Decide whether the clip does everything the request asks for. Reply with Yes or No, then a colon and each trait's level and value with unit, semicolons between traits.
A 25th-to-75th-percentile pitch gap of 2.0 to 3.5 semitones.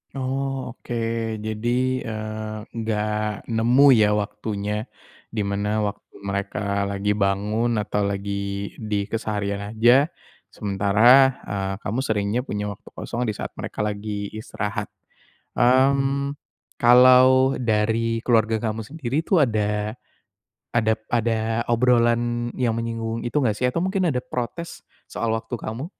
Yes: average, 2.8 semitones